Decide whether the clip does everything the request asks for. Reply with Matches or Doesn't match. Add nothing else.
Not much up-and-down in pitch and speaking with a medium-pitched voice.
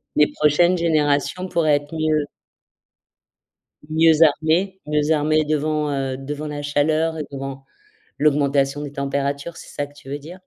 Matches